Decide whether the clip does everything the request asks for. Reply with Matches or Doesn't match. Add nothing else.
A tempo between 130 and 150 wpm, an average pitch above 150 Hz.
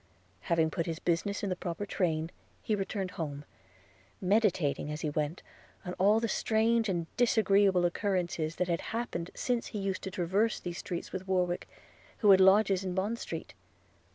Doesn't match